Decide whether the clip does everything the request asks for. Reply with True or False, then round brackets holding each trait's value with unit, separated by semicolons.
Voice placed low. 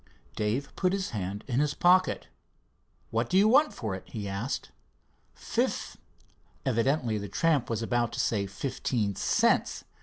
True (120 Hz)